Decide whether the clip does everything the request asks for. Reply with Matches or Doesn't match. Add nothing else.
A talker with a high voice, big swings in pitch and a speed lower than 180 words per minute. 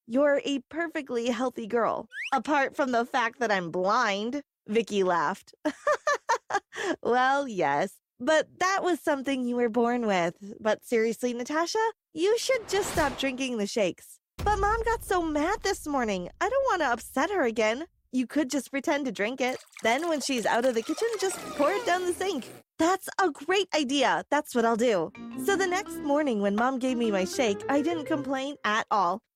Doesn't match